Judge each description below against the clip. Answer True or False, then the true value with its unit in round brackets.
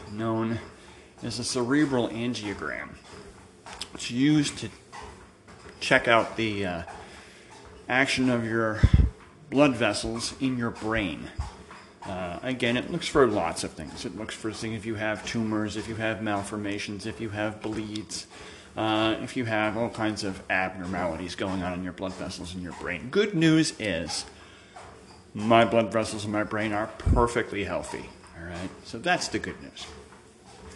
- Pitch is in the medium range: False (110 Hz)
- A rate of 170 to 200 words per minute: False (155 wpm)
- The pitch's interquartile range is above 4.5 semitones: False (2.7 semitones)